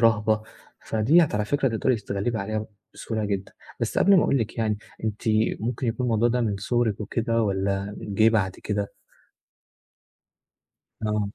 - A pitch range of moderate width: No, narrow, 2.2 semitones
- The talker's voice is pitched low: Yes, low, 110 Hz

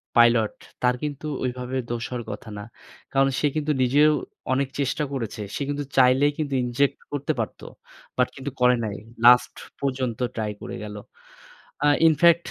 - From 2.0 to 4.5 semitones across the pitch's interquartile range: Yes, average, 2.9 semitones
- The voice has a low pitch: Yes, low, 130 Hz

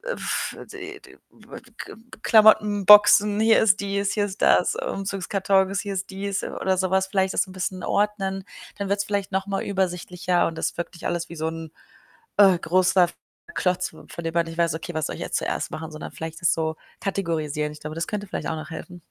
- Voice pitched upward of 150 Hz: Yes, high, 190 Hz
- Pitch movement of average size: Yes, average, 3.2 semitones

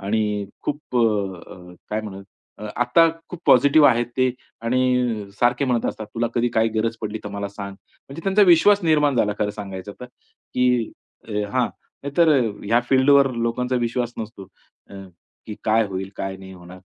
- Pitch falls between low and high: No, low, 115 Hz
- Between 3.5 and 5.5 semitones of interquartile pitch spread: Yes, average, 3.8 semitones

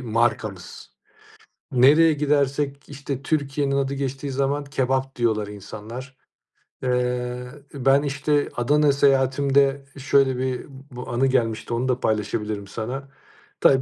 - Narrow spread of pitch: Yes, narrow, 2.2 semitones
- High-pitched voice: No, low, 135 Hz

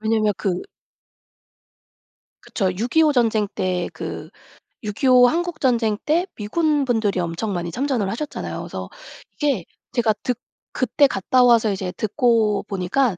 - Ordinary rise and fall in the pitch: Yes, average, 4.4 semitones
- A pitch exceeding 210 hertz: Yes, high, 225 Hz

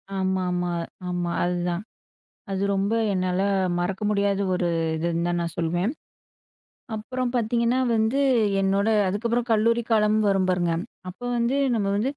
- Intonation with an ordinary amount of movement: Yes, average, 3.8 semitones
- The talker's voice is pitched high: Yes, high, 195 Hz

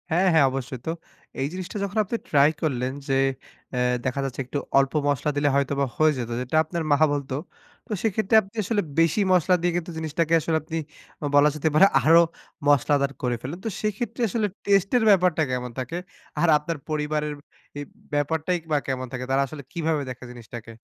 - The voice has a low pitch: No, medium, 150 Hz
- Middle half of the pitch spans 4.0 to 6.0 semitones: Yes, average, 4.5 semitones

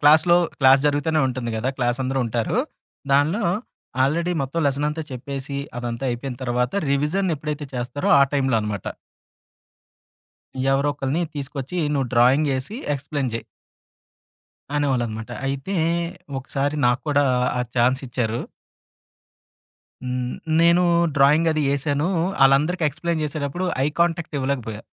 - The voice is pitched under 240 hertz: Yes, medium, 140 Hz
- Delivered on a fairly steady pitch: No, average, 3.2 semitones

